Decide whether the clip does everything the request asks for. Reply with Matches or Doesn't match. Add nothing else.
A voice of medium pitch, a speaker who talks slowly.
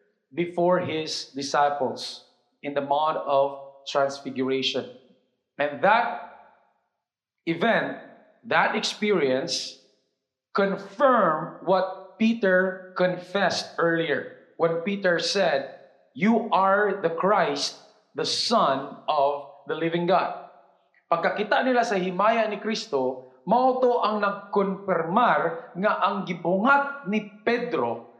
Matches